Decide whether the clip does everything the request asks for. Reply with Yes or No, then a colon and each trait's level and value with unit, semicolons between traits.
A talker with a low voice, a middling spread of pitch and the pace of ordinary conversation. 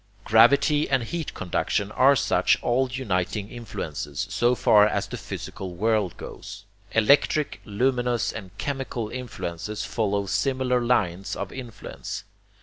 No: low, 115 Hz; average, 4.3 semitones; slow, 125 wpm